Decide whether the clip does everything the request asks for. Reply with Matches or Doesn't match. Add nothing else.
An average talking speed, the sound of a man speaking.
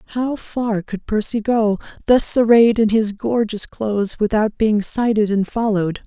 Doesn't match